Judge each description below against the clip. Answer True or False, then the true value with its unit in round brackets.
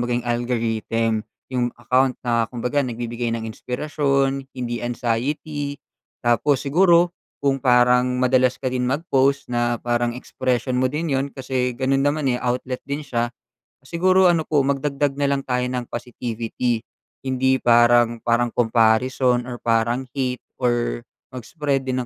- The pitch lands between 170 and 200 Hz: False (125 Hz)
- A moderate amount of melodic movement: False (2.3 semitones)